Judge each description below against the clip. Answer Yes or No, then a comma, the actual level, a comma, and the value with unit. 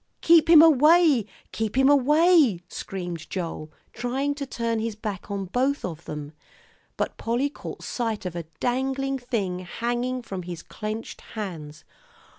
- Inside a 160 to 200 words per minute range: No, average, 145 wpm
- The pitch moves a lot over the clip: Yes, wide, 6.7 semitones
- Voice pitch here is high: Yes, high, 230 Hz